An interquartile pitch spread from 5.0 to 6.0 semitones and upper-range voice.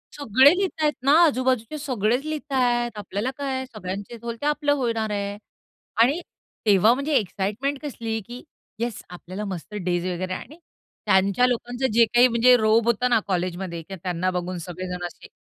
Yes: average, 5.3 semitones; high, 230 Hz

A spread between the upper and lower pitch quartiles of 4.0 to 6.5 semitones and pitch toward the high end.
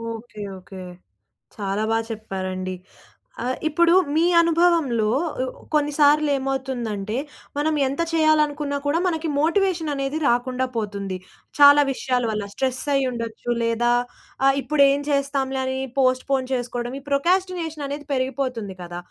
Yes: average, 4.3 semitones; very high, 265 Hz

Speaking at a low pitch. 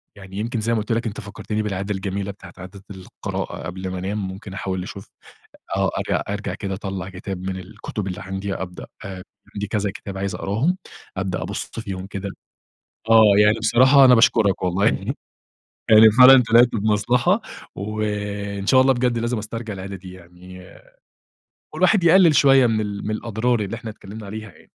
Yes: low, 105 Hz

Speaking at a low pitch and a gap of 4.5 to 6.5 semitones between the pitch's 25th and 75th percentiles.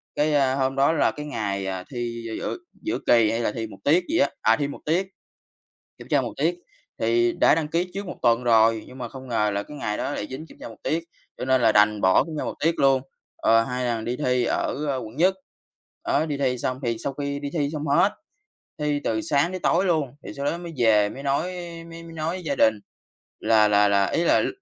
Yes: low, 130 Hz; average, 5.1 semitones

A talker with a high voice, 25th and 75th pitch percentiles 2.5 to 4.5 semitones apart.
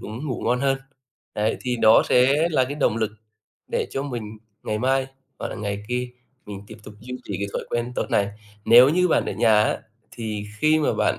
No: low, 120 Hz; average, 4.0 semitones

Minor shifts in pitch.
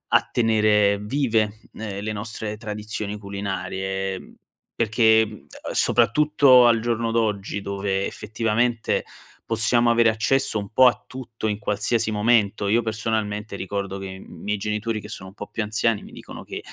Yes: narrow, 2.1 semitones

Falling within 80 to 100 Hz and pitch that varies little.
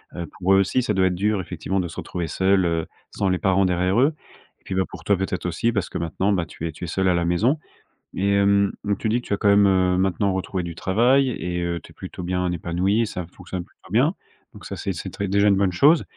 Yes: very low, 95 Hz; narrow, 2.3 semitones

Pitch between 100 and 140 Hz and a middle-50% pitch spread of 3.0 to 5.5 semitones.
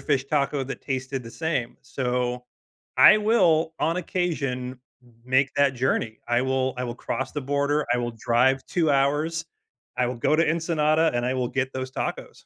Yes: low, 135 Hz; average, 3.5 semitones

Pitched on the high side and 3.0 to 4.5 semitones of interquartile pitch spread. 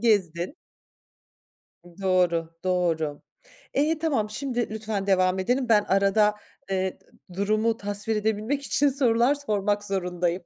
Yes: high, 205 Hz; average, 3.8 semitones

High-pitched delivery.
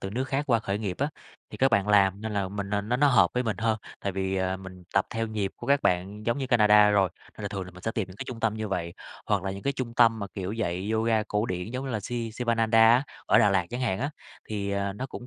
No: low, 105 Hz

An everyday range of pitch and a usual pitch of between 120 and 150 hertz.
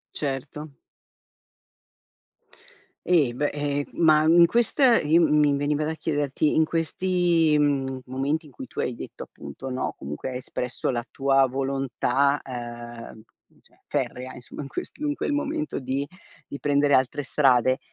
Yes: average, 3.1 semitones; medium, 140 Hz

